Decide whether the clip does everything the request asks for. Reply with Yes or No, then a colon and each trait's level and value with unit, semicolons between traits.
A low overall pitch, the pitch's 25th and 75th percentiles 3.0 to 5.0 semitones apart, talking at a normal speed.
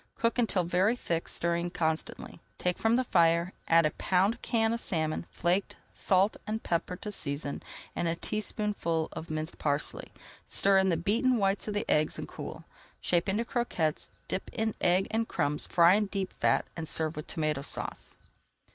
No: medium, 180 Hz; average, 4.3 semitones; average, 175 wpm